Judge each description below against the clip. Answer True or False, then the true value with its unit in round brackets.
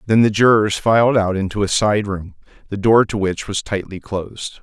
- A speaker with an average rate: False (210 wpm)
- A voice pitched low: True (105 Hz)